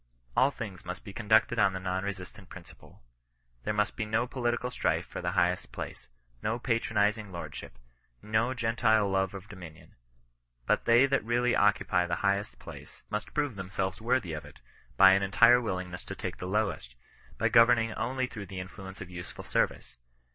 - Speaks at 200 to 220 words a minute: No, average, 175 wpm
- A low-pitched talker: Yes, low, 105 Hz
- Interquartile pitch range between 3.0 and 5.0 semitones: Yes, average, 3.7 semitones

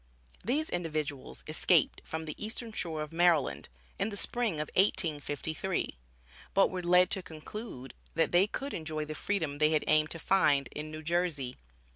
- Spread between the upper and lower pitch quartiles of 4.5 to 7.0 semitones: No, average, 3.9 semitones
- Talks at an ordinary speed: Yes, average, 165 wpm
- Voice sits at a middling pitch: Yes, medium, 165 Hz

